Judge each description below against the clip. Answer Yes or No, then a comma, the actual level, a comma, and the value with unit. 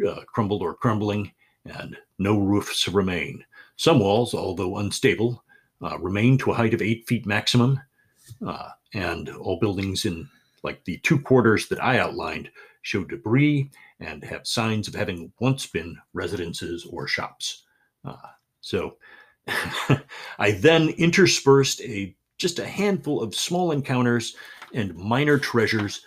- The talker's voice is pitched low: Yes, low, 115 Hz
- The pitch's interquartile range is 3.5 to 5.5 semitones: Yes, average, 5.1 semitones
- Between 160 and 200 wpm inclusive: No, average, 140 wpm